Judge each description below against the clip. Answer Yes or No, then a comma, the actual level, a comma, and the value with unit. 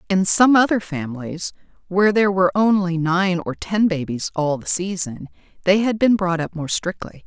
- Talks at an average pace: Yes, average, 180 wpm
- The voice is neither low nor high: Yes, medium, 180 Hz